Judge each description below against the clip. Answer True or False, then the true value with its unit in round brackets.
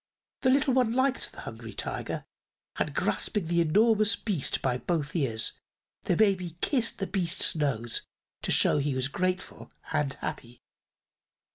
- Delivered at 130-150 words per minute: True (145 wpm)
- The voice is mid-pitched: True (175 Hz)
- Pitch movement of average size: False (7.3 semitones)